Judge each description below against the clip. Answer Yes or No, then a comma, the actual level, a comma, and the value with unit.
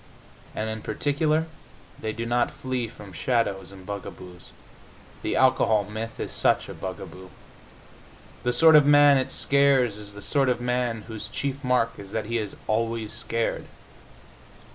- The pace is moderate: Yes, average, 155 wpm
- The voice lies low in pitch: Yes, low, 115 Hz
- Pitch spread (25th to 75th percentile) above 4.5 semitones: No, average, 3.8 semitones